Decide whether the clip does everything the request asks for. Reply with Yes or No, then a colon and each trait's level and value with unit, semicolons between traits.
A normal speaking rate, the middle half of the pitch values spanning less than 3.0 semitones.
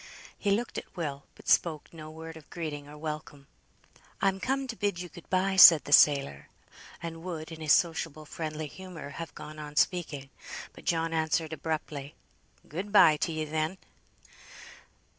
Yes: average, 165 wpm; narrow, 2.5 semitones